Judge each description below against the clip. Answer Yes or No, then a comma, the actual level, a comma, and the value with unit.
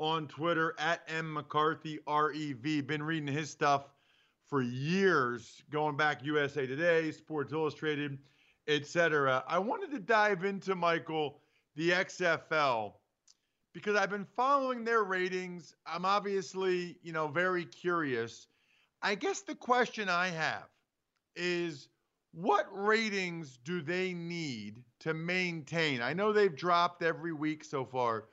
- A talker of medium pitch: Yes, medium, 165 Hz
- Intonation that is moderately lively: Yes, average, 3.5 semitones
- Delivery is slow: Yes, slow, 130 wpm